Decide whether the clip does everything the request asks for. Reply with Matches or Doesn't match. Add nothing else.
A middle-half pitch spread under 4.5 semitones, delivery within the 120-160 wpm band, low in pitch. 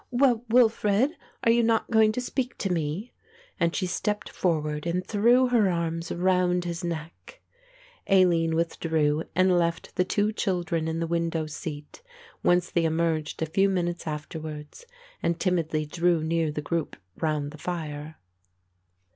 Doesn't match